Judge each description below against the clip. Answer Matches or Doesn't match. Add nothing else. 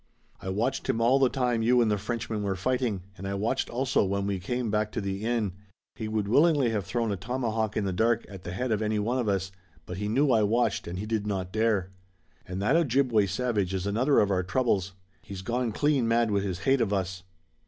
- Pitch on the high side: Doesn't match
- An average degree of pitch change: Matches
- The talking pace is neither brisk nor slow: Doesn't match